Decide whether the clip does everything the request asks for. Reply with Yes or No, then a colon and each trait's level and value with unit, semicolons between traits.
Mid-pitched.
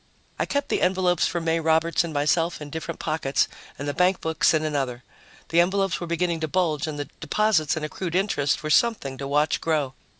Yes: medium, 160 Hz